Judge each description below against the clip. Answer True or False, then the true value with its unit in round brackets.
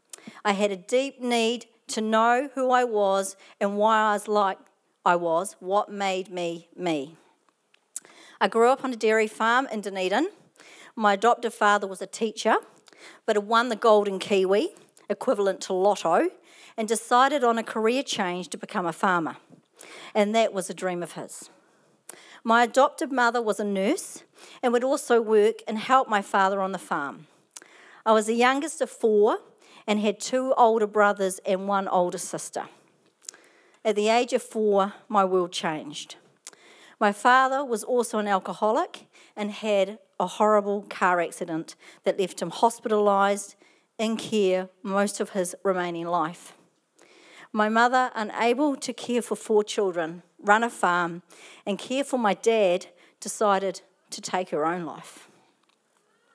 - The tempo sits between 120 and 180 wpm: True (155 wpm)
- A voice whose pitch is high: True (210 Hz)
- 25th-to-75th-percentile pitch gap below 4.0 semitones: True (3.6 semitones)